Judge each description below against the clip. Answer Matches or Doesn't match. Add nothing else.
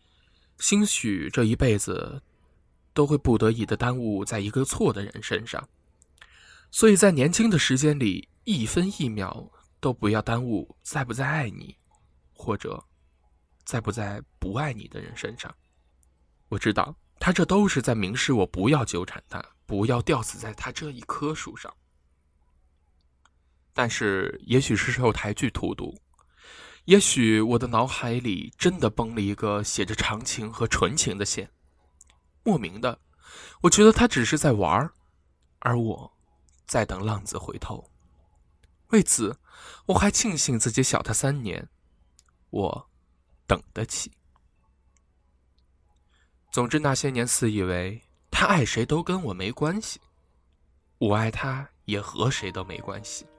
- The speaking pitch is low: Matches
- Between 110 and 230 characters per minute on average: Matches